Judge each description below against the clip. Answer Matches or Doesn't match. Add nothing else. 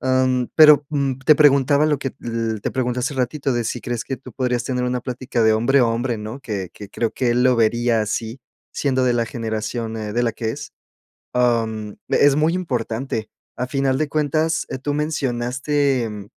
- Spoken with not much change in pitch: Doesn't match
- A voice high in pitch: Doesn't match